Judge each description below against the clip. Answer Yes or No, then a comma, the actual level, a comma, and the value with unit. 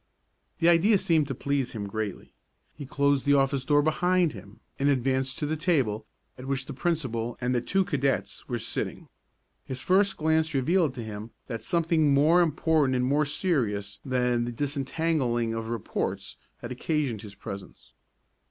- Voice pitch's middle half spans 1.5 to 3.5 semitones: No, average, 4.7 semitones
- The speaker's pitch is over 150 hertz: No, medium, 140 Hz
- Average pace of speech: Yes, average, 165 wpm